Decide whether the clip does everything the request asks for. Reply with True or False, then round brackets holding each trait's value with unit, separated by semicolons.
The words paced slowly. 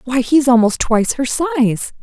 False (180 wpm)